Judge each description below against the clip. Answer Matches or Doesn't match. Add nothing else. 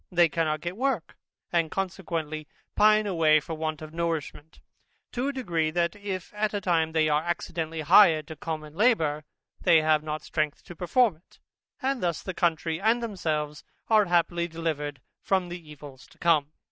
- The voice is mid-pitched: Matches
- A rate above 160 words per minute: Matches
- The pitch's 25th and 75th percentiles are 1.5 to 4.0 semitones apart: Matches